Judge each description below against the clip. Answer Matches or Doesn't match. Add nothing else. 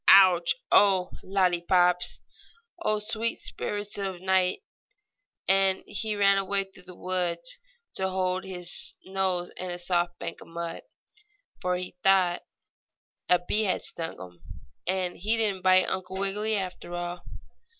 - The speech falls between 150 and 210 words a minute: Doesn't match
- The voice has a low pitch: Doesn't match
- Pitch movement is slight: Matches